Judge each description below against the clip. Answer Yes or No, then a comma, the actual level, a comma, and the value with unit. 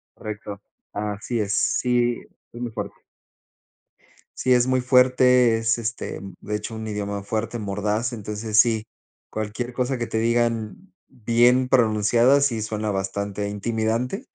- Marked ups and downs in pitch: No, narrow, 2.6 semitones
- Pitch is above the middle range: No, low, 115 Hz